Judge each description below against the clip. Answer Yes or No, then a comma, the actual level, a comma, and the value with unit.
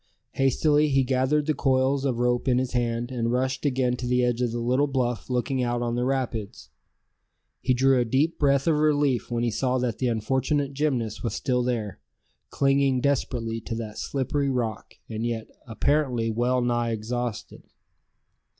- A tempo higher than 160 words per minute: Yes, average, 170 wpm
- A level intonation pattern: Yes, narrow, 2.2 semitones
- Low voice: Yes, low, 125 Hz